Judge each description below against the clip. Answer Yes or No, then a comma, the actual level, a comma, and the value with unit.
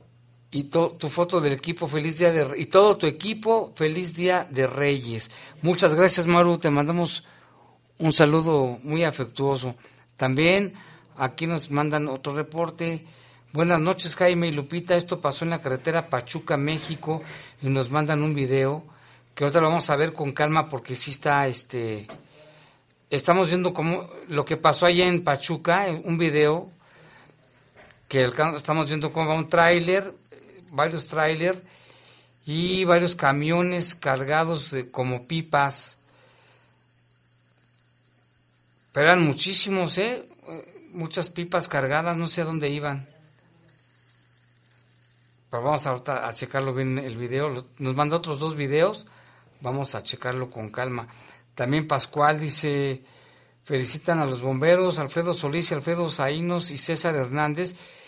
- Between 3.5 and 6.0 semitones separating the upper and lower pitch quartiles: Yes, average, 4.2 semitones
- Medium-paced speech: Yes, average, 135 wpm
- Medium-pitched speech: Yes, medium, 150 Hz